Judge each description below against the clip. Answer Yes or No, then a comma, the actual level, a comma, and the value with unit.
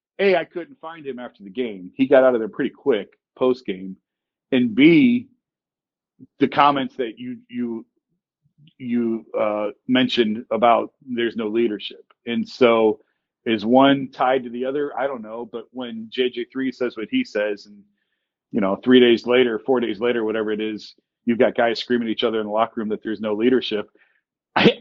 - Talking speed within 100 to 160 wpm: No, average, 185 wpm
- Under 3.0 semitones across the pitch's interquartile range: No, average, 3.7 semitones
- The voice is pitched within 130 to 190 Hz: No, low, 120 Hz